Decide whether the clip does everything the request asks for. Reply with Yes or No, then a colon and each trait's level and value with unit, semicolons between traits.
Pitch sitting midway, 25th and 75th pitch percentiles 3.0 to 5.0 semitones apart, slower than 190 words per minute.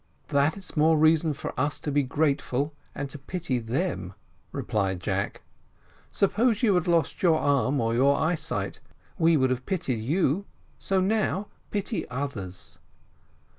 No: medium, 145 Hz; wide, 5.5 semitones; average, 140 wpm